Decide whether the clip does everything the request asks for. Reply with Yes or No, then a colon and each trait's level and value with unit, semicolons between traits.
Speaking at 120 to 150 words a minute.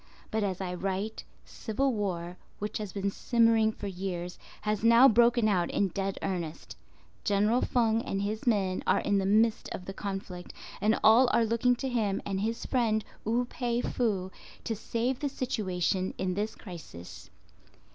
No: average, 165 wpm